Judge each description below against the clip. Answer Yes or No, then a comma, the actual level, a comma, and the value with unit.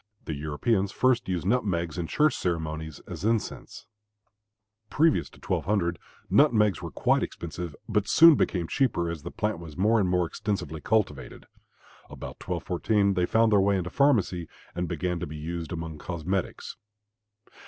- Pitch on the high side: No, very low, 90 Hz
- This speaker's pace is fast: No, average, 155 wpm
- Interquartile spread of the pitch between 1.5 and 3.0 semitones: No, average, 4.2 semitones